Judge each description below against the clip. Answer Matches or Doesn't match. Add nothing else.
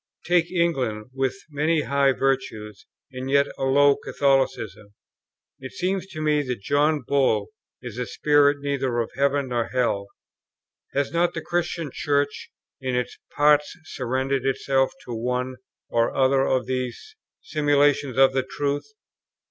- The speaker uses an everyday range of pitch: Doesn't match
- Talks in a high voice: Doesn't match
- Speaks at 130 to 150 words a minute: Matches